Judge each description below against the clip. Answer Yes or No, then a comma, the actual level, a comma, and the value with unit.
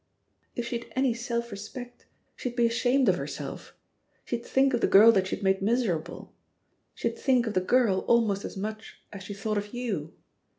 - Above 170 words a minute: Yes, average, 185 wpm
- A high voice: Yes, high, 230 Hz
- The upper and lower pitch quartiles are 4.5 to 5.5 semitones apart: No, average, 3.4 semitones